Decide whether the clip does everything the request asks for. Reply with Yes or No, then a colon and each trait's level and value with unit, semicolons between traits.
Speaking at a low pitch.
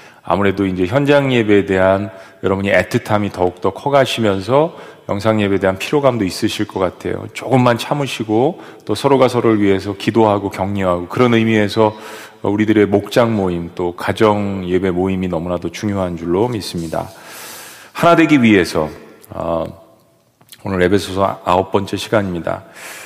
Yes: low, 100 Hz